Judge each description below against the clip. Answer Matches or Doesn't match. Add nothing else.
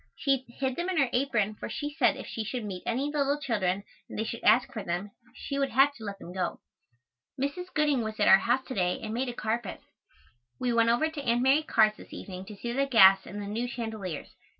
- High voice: Matches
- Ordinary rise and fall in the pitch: Matches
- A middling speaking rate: Doesn't match